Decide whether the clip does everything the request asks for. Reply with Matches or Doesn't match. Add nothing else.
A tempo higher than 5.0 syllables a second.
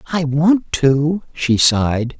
Doesn't match